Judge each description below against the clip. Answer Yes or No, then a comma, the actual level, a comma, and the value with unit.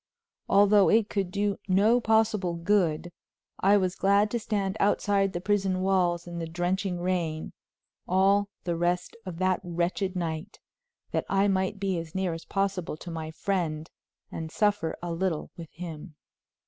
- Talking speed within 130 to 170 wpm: Yes, average, 160 wpm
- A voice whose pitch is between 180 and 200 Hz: Yes, medium, 185 Hz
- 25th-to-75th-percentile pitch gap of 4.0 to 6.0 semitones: No, average, 2.7 semitones